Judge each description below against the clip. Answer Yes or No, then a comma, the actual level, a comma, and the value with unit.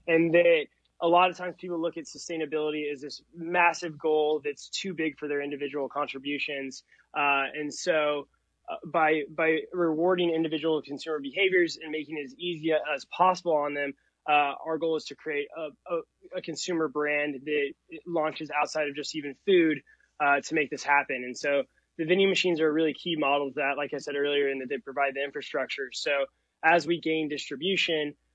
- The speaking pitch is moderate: Yes, medium, 155 Hz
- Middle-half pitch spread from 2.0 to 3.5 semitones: Yes, narrow, 2.5 semitones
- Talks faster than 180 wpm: Yes, average, 190 wpm